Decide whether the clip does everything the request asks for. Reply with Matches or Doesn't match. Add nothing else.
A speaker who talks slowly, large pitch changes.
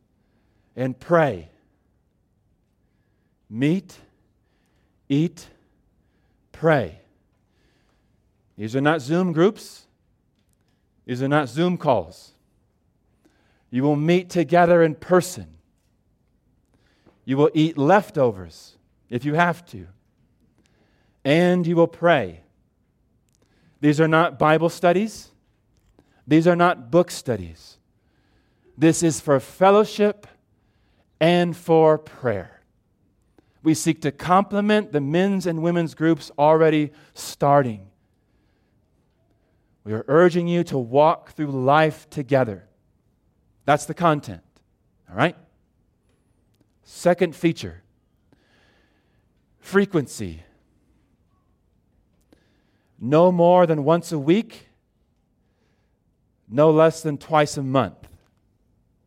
Matches